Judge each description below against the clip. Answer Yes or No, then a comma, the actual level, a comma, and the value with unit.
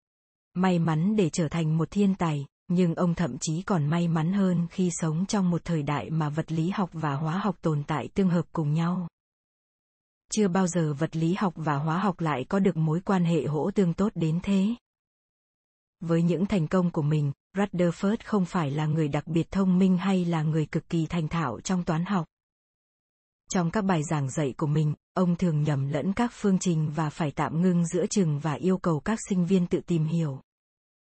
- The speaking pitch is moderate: Yes, medium, 170 Hz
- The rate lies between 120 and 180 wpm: No, average, 210 wpm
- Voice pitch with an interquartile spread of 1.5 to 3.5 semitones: Yes, average, 3.0 semitones